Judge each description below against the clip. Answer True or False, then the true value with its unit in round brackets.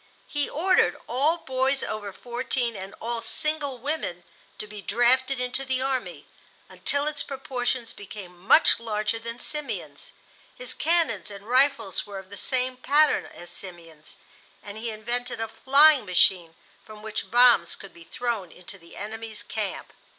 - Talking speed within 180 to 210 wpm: False (150 wpm)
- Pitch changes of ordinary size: True (4.7 semitones)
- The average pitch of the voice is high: True (235 Hz)